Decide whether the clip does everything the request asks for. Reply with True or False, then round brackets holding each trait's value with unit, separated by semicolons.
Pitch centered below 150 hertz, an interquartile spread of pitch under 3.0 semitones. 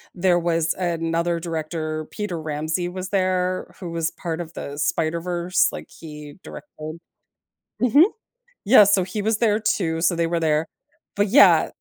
False (170 Hz; 2.5 semitones)